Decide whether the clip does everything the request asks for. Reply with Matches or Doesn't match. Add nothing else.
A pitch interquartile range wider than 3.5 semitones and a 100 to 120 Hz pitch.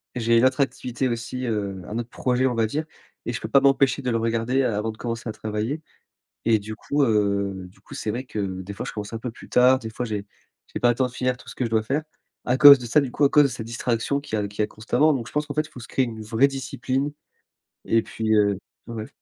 Doesn't match